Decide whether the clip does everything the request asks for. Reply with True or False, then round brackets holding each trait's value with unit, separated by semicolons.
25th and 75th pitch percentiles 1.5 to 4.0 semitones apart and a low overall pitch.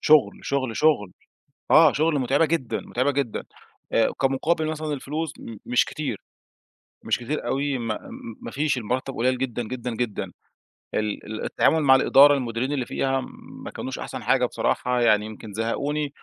True (3.6 semitones; 130 Hz)